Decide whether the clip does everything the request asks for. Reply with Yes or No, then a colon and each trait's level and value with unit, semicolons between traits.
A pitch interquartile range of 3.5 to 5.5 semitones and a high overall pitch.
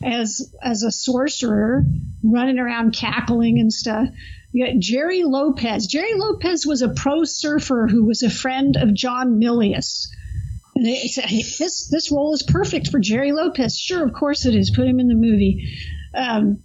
Yes: average, 4.2 semitones; high, 245 Hz